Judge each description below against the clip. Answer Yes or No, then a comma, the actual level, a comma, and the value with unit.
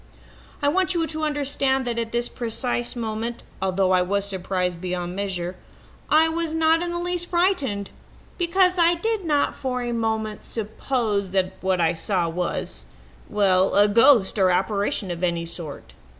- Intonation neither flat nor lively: No, wide, 8.4 semitones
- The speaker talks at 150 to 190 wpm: Yes, average, 165 wpm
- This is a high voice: Yes, high, 220 Hz